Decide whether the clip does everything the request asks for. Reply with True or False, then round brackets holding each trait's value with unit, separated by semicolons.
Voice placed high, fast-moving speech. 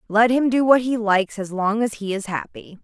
True (215 Hz; 255 wpm)